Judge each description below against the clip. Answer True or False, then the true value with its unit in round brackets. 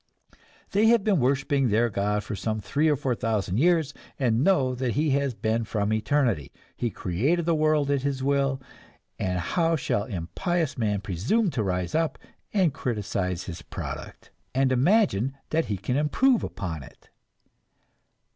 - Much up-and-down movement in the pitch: True (6.9 semitones)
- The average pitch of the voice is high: False (130 Hz)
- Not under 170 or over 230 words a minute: False (160 wpm)